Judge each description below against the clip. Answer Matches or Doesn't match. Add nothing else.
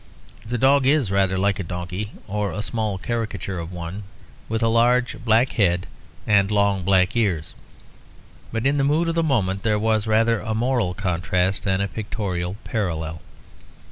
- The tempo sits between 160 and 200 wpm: Matches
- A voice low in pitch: Matches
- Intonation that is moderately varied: Matches